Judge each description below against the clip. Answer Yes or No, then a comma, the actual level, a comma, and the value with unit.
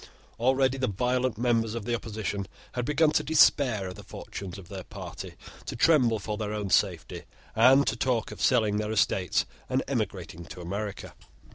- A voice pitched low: Yes, low, 110 Hz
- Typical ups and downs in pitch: Yes, average, 3.8 semitones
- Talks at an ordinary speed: Yes, average, 175 wpm